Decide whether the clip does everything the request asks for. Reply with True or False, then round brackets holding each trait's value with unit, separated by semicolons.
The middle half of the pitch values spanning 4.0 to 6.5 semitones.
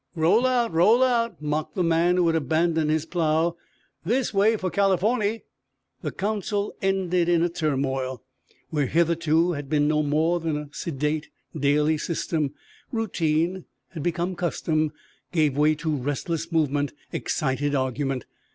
False (3.3 semitones)